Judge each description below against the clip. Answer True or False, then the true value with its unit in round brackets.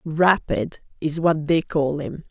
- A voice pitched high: False (160 Hz)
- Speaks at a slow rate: False (155 wpm)